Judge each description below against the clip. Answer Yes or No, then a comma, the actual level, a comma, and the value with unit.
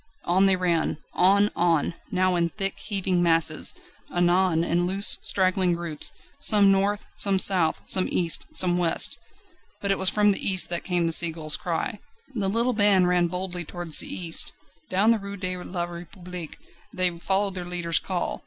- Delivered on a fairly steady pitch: Yes, narrow, 2.0 semitones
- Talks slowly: No, average, 170 wpm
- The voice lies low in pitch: No, medium, 180 Hz